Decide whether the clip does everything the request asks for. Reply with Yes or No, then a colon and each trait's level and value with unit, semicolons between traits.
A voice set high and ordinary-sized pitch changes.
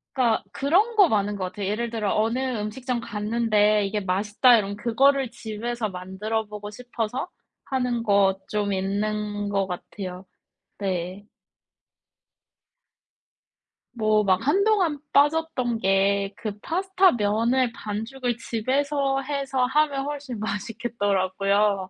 Yes: high, 220 Hz; average, 4.2 semitones